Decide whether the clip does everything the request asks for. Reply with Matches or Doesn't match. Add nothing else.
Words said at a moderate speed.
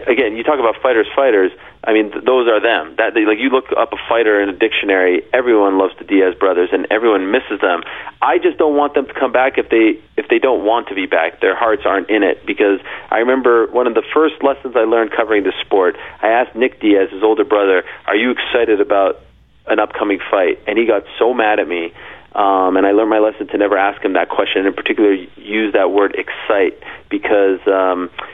Doesn't match